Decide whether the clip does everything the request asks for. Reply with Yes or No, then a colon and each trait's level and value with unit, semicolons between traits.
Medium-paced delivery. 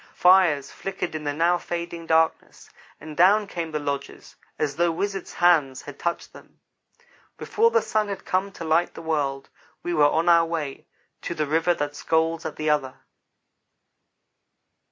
Yes: average, 165 wpm